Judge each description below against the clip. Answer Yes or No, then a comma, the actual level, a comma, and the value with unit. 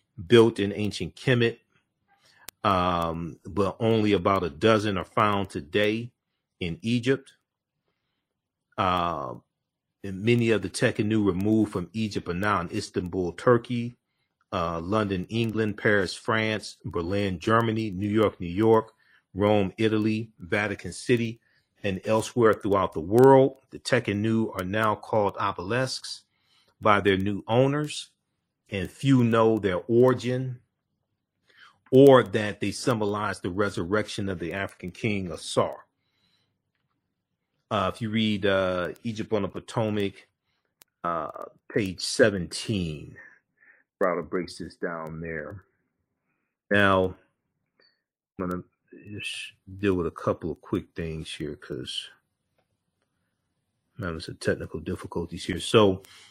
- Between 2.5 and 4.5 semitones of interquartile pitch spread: Yes, average, 3.1 semitones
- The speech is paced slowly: Yes, slow, 120 wpm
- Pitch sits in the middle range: No, low, 105 Hz